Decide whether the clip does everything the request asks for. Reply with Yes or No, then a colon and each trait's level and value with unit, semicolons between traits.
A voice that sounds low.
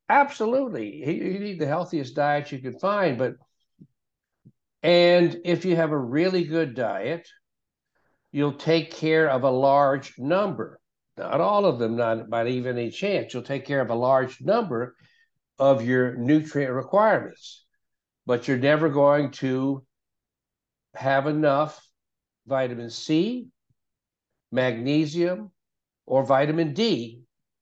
No: medium, 145 Hz